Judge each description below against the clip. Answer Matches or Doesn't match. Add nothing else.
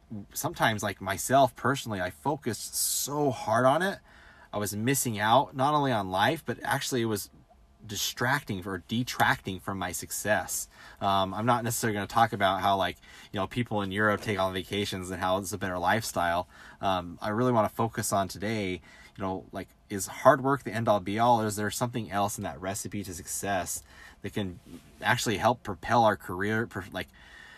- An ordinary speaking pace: Matches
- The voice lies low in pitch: Matches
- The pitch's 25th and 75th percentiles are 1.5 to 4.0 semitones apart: Matches